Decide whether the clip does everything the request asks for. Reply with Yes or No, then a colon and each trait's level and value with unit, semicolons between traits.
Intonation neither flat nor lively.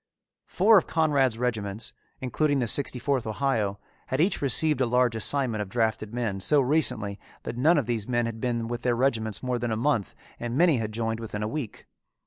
Yes: average, 3.7 semitones